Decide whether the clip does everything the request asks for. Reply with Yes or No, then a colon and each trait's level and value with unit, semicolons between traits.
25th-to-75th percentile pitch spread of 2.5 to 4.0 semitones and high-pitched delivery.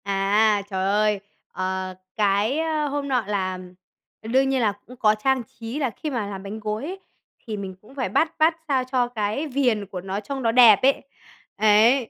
No: average, 4.8 semitones; high, 220 Hz